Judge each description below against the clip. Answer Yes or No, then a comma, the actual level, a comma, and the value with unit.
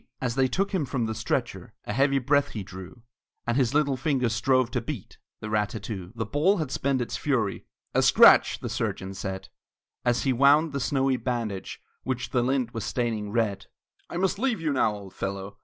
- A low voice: Yes, low, 125 Hz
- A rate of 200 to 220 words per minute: Yes, fast, 205 wpm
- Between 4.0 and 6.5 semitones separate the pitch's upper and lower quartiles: Yes, average, 4.4 semitones